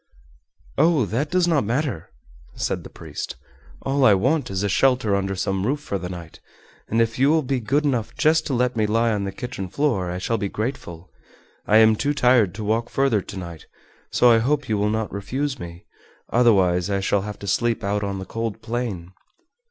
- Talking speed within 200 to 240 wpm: Yes, fast, 205 wpm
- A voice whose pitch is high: No, low, 110 Hz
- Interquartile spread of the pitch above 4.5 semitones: Yes, average, 5.0 semitones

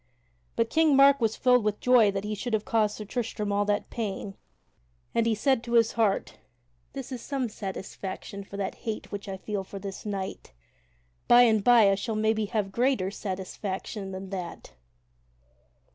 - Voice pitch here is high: Yes, high, 210 Hz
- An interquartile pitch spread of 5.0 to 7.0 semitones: No, average, 3.0 semitones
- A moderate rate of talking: Yes, average, 175 wpm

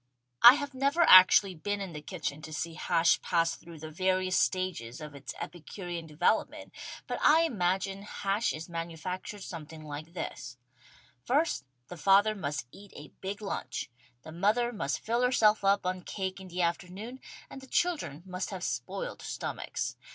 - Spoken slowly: No, average, 165 wpm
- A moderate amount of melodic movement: Yes, average, 4.1 semitones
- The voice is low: No, medium, 185 Hz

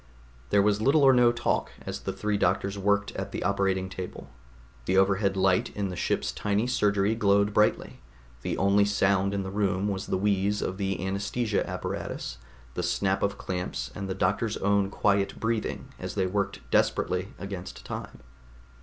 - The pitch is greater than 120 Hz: No, low, 100 Hz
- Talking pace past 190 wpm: No, average, 170 wpm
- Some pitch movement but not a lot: No, narrow, 1.3 semitones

